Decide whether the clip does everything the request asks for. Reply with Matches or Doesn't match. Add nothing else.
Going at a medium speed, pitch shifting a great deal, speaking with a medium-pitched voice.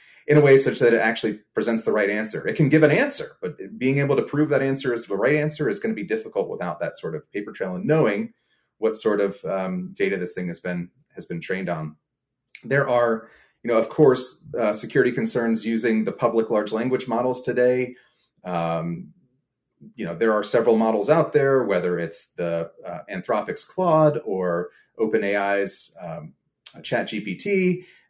Doesn't match